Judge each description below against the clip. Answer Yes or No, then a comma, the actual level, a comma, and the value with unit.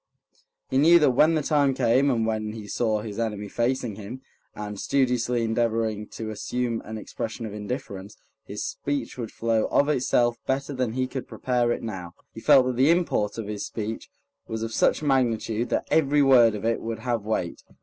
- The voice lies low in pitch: Yes, low, 115 Hz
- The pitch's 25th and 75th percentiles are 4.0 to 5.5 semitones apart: No, average, 3.1 semitones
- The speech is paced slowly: No, average, 190 wpm